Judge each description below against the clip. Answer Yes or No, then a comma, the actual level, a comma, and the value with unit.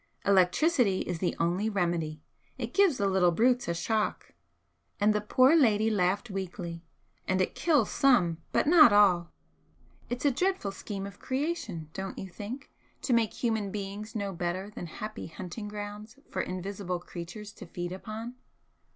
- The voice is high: Yes, high, 205 Hz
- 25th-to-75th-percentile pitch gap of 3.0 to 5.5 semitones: Yes, average, 4.1 semitones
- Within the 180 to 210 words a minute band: No, average, 160 wpm